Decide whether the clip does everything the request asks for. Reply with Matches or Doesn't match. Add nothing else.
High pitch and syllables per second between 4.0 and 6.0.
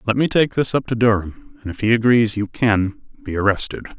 Doesn't match